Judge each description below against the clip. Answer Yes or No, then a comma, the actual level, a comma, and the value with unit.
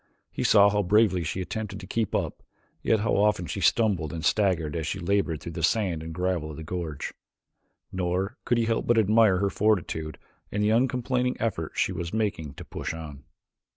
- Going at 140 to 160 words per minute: No, average, 195 wpm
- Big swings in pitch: No, average, 4.9 semitones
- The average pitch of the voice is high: No, very low, 95 Hz